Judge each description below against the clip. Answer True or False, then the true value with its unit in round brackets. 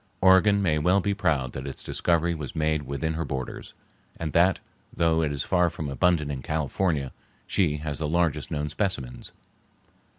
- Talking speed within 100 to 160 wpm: False (170 wpm)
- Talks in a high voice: False (80 Hz)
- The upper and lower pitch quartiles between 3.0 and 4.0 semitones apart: True (3.4 semitones)